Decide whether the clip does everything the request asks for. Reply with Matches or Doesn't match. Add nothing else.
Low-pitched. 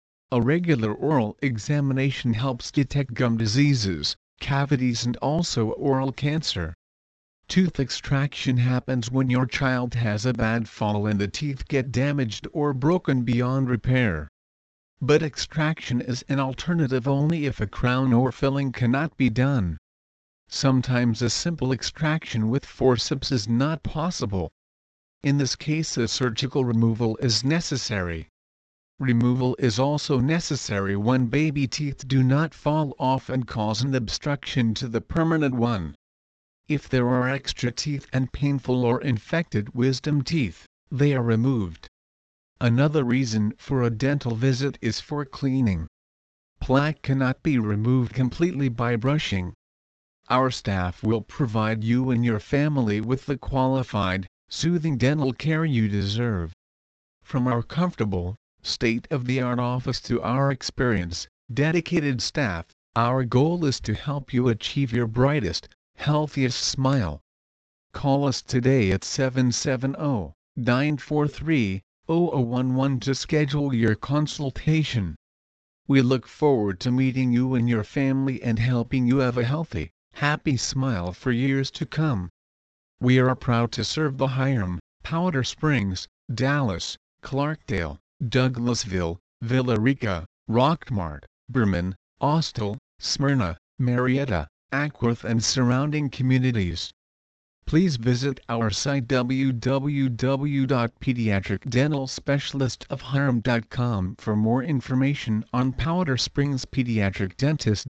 Matches